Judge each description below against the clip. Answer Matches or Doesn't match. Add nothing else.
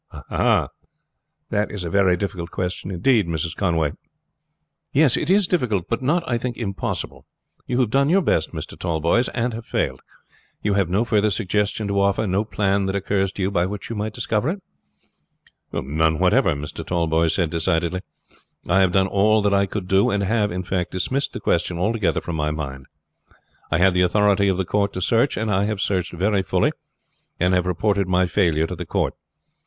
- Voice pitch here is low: Matches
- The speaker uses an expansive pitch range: Doesn't match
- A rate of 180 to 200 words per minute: Matches